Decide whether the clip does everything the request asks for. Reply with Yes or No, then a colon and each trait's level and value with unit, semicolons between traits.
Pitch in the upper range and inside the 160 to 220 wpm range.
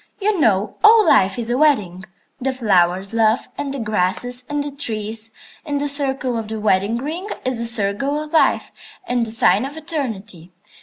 Yes: high, 240 Hz; average, 185 wpm